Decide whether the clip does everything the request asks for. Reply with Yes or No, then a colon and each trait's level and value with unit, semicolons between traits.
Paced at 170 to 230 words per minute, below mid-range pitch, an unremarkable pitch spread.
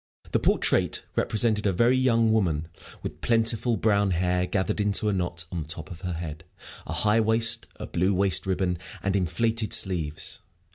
Yes: average, 175 wpm; very low, 95 Hz; average, 4.1 semitones